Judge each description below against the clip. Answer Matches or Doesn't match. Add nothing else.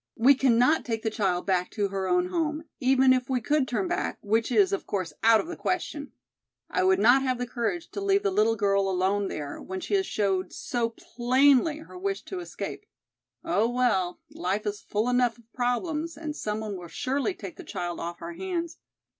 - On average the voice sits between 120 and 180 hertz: Doesn't match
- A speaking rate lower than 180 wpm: Doesn't match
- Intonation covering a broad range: Matches